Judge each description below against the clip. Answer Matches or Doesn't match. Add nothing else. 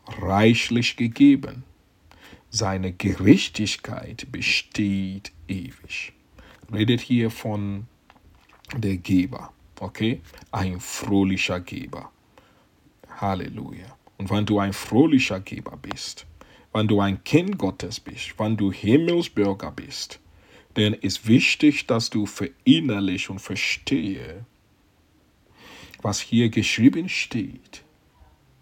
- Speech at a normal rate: Doesn't match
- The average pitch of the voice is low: Matches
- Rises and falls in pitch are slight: Doesn't match